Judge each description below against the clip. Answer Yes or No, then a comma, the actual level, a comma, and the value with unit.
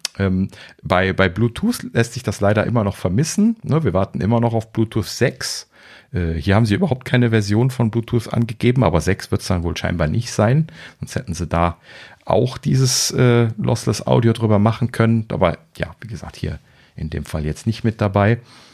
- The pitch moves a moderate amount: Yes, average, 3.6 semitones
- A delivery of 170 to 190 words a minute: Yes, average, 185 wpm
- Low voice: Yes, low, 110 Hz